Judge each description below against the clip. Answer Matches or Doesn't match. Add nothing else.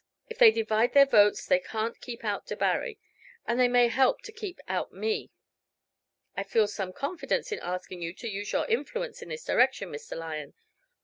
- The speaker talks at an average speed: Matches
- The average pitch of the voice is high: Matches